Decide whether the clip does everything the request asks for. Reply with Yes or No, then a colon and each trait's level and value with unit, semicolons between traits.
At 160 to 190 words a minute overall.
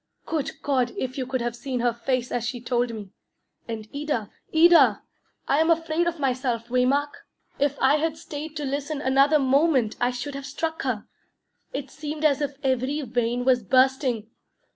Yes: average, 175 wpm